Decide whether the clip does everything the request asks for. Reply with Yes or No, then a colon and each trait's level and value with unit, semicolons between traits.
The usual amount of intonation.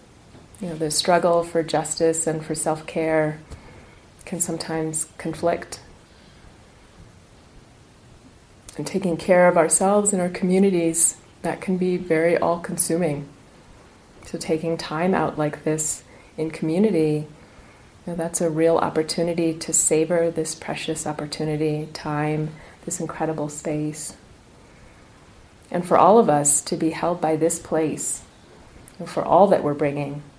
No: narrow, 1.6 semitones